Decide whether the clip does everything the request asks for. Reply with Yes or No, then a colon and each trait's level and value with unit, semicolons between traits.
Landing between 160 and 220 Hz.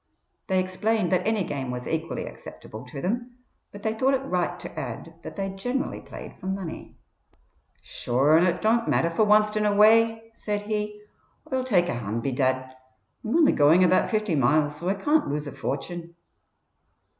Yes: high, 190 Hz